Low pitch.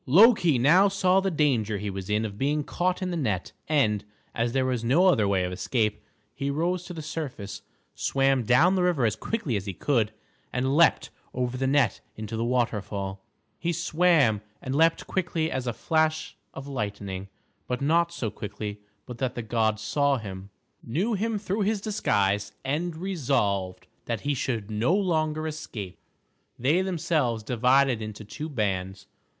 Yes: low, 130 Hz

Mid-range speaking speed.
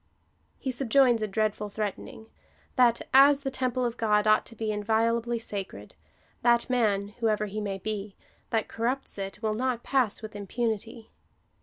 Yes: average, 160 wpm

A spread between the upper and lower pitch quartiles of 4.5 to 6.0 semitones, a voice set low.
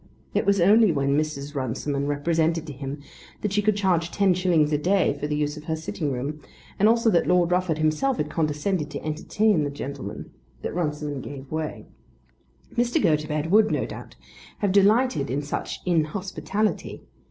No: average, 4.8 semitones; medium, 160 Hz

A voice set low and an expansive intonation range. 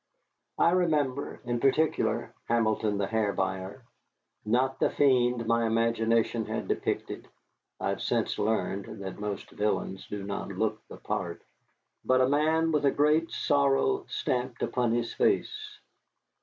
No: low, 120 Hz; average, 4.8 semitones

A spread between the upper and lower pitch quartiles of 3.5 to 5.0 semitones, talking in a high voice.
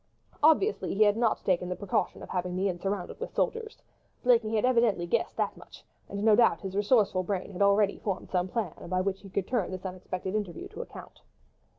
No: average, 3.0 semitones; high, 200 Hz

